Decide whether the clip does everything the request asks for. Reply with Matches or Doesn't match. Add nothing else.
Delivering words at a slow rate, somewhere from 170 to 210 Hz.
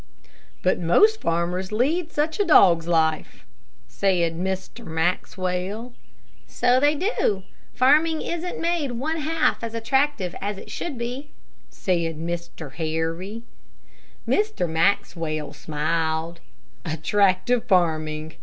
Matches